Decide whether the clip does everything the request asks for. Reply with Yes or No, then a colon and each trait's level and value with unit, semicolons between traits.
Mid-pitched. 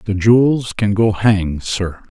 No: low, 105 Hz